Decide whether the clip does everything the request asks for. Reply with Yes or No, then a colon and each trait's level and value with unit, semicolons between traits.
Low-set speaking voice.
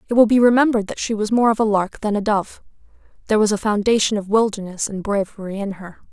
No: high, 210 Hz